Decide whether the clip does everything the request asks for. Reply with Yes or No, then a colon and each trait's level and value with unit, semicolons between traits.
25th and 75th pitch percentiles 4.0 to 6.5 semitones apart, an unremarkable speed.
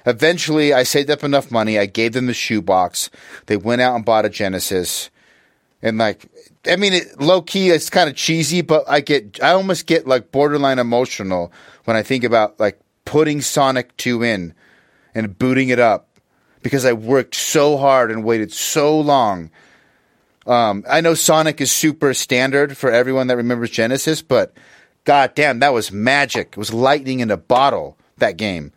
Yes: average, 4.9 semitones; average, 175 wpm